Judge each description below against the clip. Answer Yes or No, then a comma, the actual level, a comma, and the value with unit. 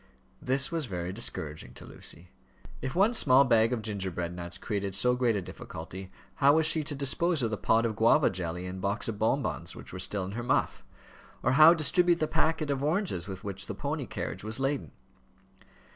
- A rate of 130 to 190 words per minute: No, average, 200 wpm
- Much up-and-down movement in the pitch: Yes, wide, 7.0 semitones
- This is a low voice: Yes, low, 115 Hz